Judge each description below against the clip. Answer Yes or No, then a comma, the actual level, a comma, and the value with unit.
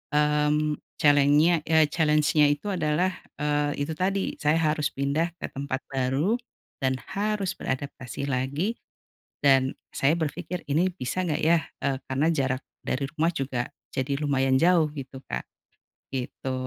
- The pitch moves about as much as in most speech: Yes, average, 3.1 semitones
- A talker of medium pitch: Yes, medium, 150 Hz